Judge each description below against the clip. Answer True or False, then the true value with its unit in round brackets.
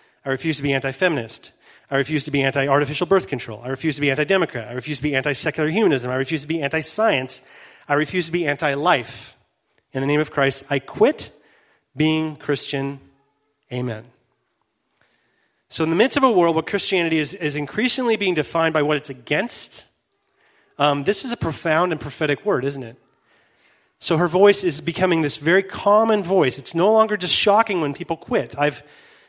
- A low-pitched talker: False (150 Hz)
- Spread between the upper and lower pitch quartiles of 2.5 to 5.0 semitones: True (4.6 semitones)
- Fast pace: False (195 wpm)